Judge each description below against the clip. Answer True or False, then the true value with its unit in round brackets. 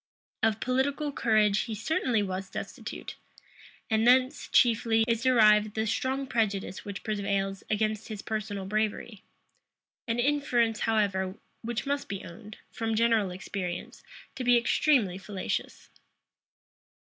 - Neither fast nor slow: False (120 wpm)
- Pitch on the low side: False (220 Hz)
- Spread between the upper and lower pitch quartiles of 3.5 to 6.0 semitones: False (2.9 semitones)